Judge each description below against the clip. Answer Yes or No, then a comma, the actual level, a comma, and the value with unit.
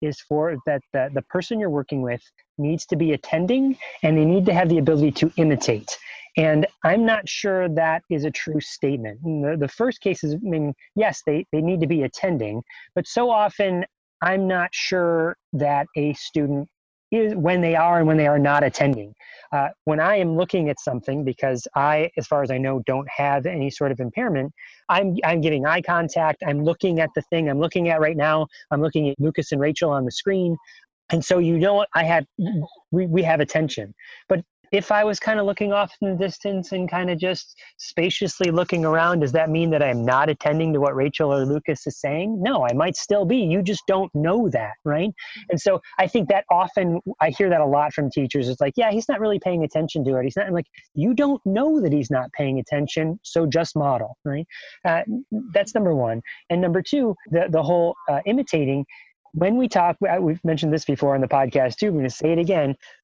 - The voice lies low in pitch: No, medium, 160 Hz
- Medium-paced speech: No, fast, 220 wpm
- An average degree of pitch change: Yes, average, 4.2 semitones